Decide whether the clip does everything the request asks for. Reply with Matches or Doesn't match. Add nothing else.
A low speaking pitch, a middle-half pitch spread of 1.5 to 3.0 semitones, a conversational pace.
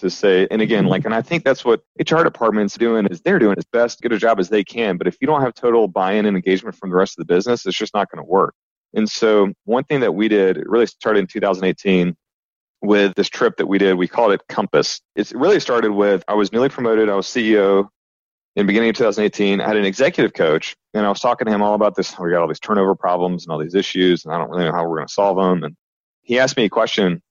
Doesn't match